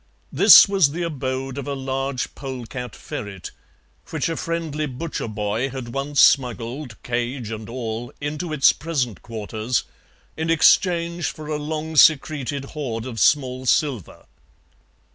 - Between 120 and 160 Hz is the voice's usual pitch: Yes, low, 135 Hz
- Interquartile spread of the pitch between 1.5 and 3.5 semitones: No, average, 4.2 semitones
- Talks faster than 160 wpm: No, slow, 135 wpm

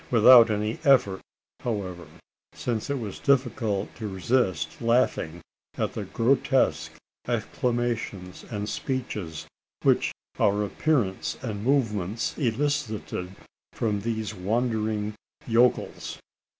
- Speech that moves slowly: Yes, slow, 100 wpm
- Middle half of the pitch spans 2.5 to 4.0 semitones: Yes, average, 3.4 semitones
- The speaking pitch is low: Yes, low, 110 Hz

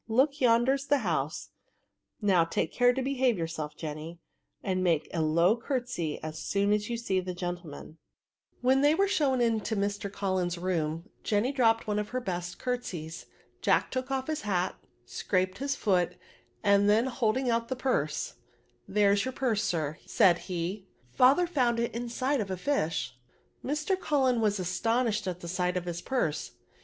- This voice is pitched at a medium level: No, high, 205 Hz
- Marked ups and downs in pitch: Yes, wide, 6.2 semitones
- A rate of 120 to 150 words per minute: No, average, 180 wpm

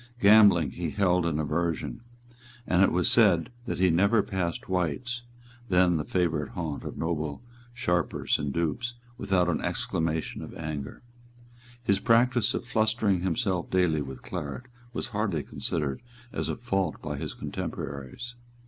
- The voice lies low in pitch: Yes, very low, 90 Hz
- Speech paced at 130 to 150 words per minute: Yes, average, 145 wpm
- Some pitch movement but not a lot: Yes, average, 4.8 semitones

